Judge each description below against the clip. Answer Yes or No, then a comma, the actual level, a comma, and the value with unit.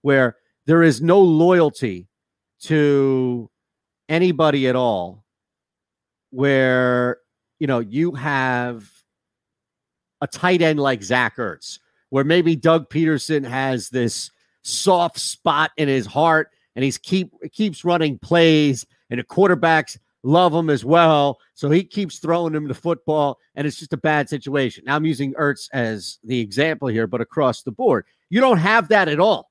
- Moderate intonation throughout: Yes, average, 4.6 semitones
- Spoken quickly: No, average, 155 wpm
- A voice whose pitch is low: No, medium, 145 Hz